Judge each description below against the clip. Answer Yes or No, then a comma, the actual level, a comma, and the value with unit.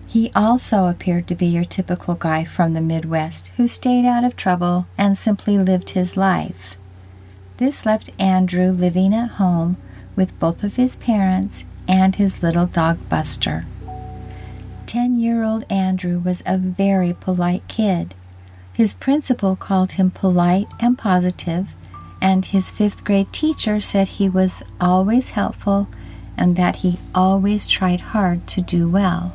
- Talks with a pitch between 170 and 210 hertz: Yes, medium, 185 Hz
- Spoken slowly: No, average, 145 wpm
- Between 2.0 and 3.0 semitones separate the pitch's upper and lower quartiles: Yes, narrow, 2.5 semitones